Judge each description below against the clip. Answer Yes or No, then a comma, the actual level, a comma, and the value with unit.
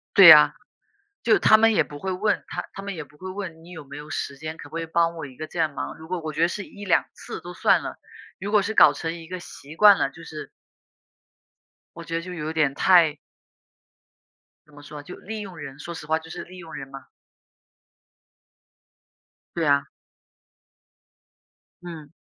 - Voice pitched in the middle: Yes, medium, 165 Hz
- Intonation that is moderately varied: Yes, average, 3.3 semitones